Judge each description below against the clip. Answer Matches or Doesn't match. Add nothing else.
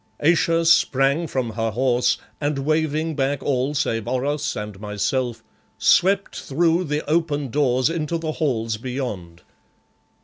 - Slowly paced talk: Matches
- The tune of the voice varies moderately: Matches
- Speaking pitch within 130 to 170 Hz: Matches